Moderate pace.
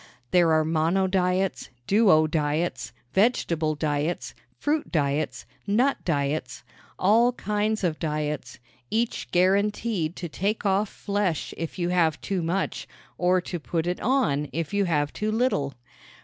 No: slow, 130 wpm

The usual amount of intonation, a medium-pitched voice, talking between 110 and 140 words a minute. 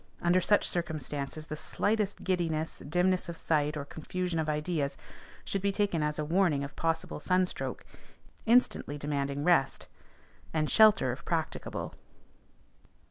Yes: average, 3.6 semitones; medium, 160 Hz; slow, 135 wpm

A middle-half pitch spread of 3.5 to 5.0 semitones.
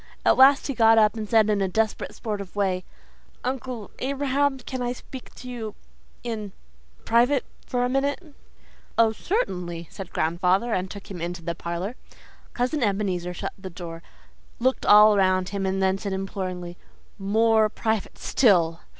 Yes: average, 4.7 semitones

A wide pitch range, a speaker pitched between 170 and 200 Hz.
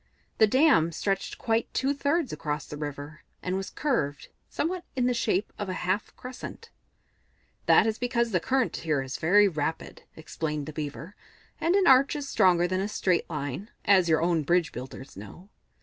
Yes: wide, 7.9 semitones; medium, 185 Hz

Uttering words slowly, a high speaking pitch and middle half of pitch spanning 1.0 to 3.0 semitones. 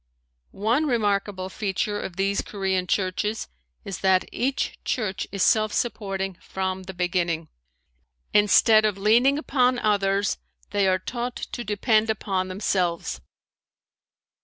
Yes: slow, 120 wpm; high, 200 Hz; narrow, 2.5 semitones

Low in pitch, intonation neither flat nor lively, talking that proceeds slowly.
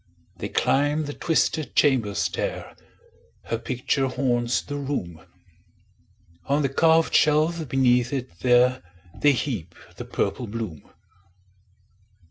Yes: low, 130 Hz; average, 3.4 semitones; slow, 110 wpm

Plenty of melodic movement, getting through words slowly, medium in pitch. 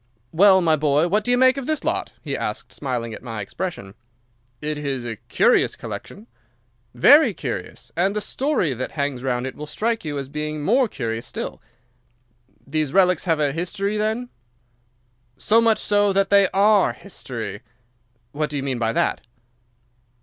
No: wide, 7.3 semitones; average, 170 wpm; medium, 160 Hz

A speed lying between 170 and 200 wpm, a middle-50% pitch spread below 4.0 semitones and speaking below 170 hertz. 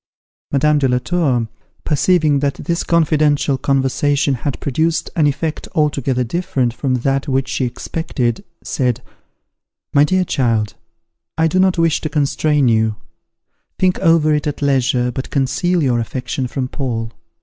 No: average, 145 wpm; average, 3.5 semitones; medium, 140 Hz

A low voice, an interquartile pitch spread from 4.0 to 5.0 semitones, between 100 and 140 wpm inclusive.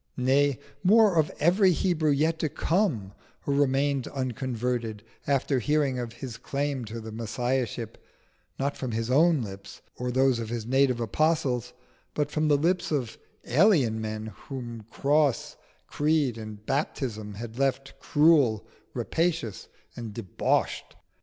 Yes: low, 130 Hz; average, 4.4 semitones; slow, 135 wpm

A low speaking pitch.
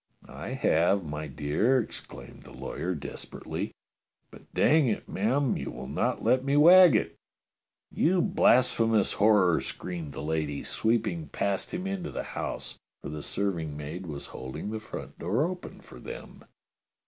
Yes: low, 105 Hz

